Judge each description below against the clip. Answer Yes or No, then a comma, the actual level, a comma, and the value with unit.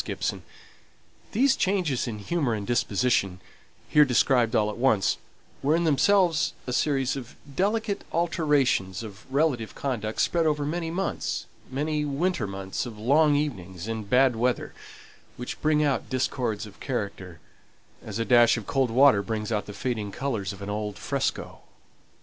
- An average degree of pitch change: No, wide, 5.9 semitones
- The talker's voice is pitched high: No, low, 125 Hz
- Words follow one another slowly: No, average, 150 wpm